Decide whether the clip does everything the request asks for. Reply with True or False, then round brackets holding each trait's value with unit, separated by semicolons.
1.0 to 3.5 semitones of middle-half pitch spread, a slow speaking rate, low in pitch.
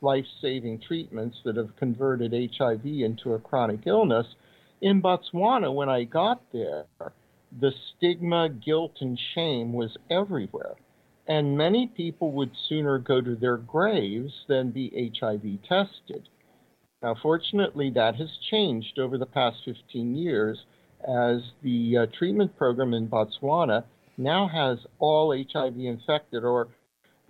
False (4.7 semitones; 130 wpm; 130 Hz)